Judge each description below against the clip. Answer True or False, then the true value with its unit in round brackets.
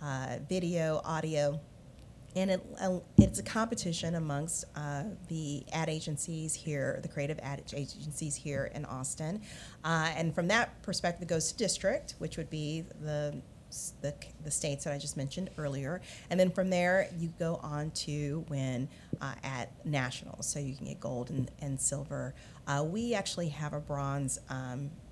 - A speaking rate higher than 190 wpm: False (165 wpm)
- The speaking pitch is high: False (150 Hz)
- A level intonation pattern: False (3.3 semitones)